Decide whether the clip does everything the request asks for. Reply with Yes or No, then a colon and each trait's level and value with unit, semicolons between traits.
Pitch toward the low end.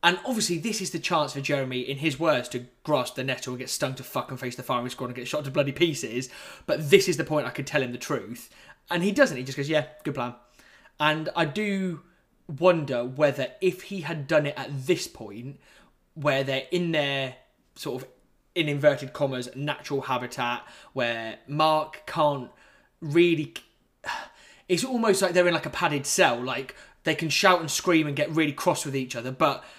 No: medium, 150 Hz